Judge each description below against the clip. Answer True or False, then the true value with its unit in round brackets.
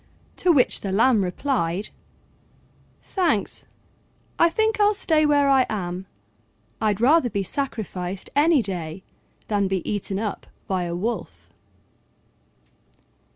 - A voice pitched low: False (215 Hz)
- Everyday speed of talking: False (115 wpm)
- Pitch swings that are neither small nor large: False (7.2 semitones)